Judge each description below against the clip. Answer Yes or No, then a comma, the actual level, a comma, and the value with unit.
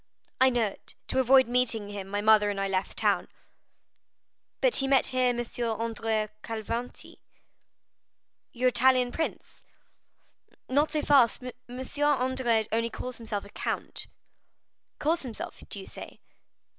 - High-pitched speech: Yes, high, 245 Hz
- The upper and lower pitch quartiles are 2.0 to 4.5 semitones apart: Yes, average, 3.0 semitones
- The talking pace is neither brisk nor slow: No, slow, 130 wpm